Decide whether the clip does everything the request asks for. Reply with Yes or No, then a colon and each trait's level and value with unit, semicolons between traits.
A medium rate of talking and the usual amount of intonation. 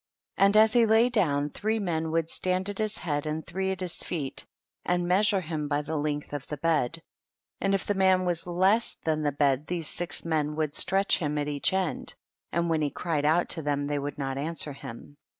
No: fast, 220 wpm; average, 4.3 semitones